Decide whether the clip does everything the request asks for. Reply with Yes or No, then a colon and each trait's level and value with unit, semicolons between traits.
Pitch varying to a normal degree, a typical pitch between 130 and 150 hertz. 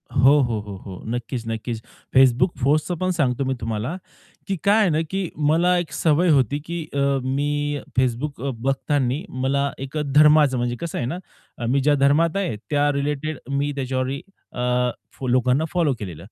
Yes: average, 3.6 semitones; medium, 140 Hz